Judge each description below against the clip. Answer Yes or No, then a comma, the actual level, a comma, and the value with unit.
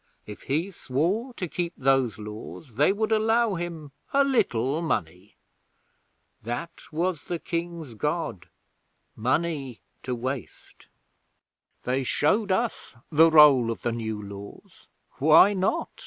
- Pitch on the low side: No, medium, 150 Hz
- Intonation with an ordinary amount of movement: No, wide, 6.5 semitones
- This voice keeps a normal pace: No, slow, 125 wpm